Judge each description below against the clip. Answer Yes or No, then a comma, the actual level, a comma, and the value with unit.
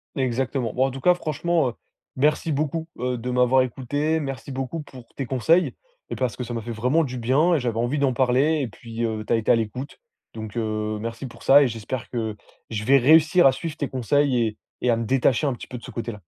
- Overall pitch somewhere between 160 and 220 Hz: No, low, 130 Hz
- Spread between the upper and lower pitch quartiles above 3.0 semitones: Yes, average, 3.6 semitones